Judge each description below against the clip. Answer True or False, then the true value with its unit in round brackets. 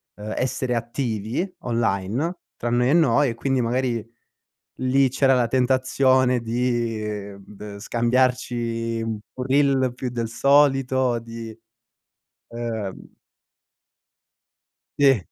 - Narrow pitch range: True (2.3 semitones)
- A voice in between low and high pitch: False (120 Hz)